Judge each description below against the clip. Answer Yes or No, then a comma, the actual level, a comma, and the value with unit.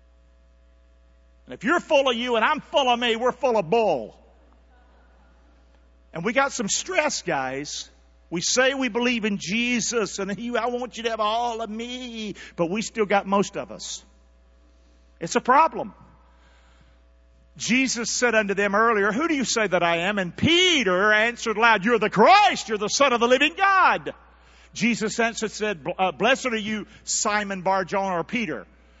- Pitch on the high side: Yes, high, 210 Hz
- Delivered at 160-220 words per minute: Yes, average, 175 wpm